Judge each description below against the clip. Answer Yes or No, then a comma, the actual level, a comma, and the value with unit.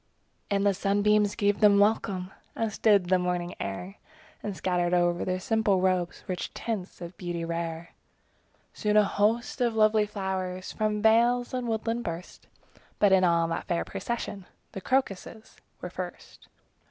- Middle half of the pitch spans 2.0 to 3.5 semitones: Yes, average, 3.1 semitones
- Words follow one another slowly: No, average, 155 wpm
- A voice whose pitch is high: Yes, high, 200 Hz